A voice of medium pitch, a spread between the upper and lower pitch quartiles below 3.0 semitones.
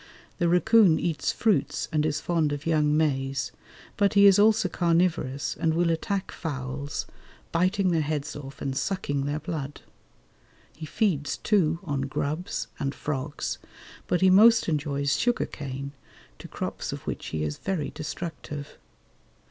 No: medium, 155 Hz; average, 4.1 semitones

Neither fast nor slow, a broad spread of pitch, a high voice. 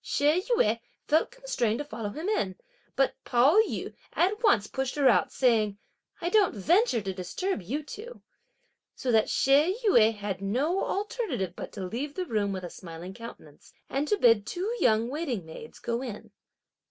Yes: average, 175 wpm; wide, 9.0 semitones; very high, 255 Hz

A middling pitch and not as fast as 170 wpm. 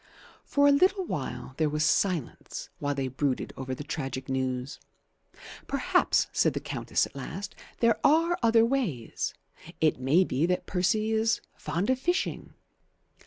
Yes: medium, 170 Hz; average, 150 wpm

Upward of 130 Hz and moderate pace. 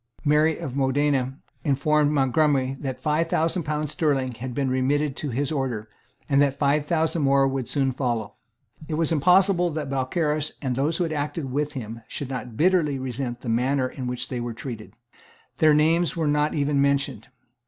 Yes: medium, 140 Hz; average, 180 wpm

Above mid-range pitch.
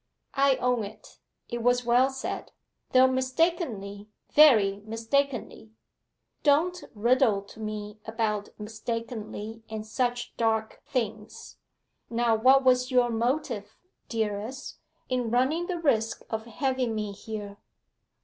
Yes: high, 230 Hz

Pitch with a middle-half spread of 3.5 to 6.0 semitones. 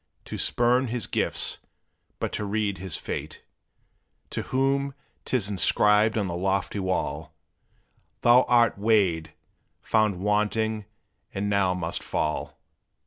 No: average, 3.0 semitones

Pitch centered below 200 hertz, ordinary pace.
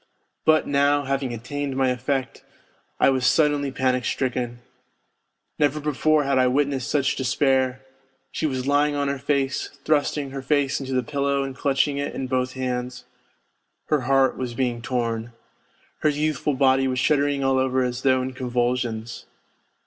Yes: low, 135 Hz; average, 155 wpm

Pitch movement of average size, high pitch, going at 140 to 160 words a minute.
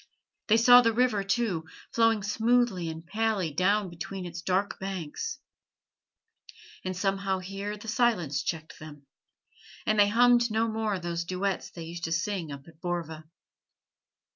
Yes: average, 4.7 semitones; high, 195 Hz; average, 145 wpm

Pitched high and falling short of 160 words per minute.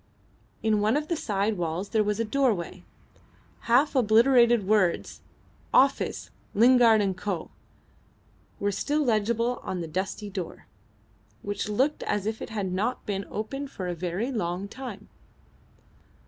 Yes: high, 215 Hz; average, 140 wpm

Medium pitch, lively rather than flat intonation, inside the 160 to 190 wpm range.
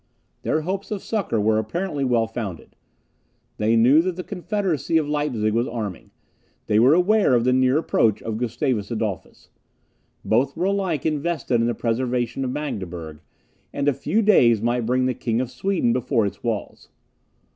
No: low, 125 Hz; wide, 5.8 semitones; average, 170 wpm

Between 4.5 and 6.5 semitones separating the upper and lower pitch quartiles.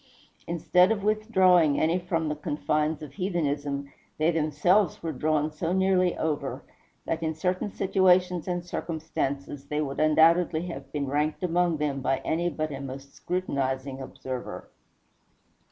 No: average, 3.6 semitones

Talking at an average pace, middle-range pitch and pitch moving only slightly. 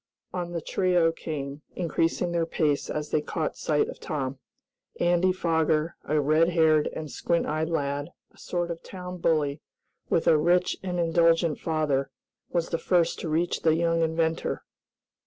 Yes: average, 160 wpm; medium, 165 Hz; narrow, 2.0 semitones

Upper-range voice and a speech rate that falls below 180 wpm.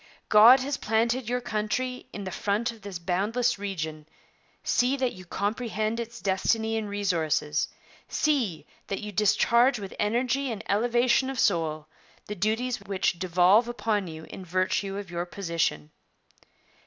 Yes: high, 210 Hz; average, 145 wpm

